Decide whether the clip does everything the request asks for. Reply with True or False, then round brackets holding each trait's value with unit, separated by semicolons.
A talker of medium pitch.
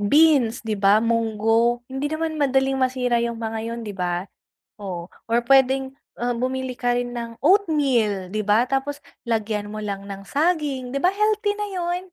False (245 Hz)